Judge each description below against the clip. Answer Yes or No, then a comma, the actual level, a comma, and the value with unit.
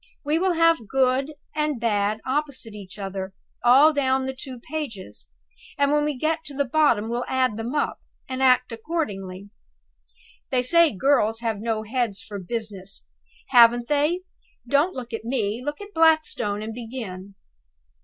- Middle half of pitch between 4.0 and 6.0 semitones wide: Yes, average, 5.2 semitones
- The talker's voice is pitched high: Yes, very high, 250 Hz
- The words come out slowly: No, average, 155 wpm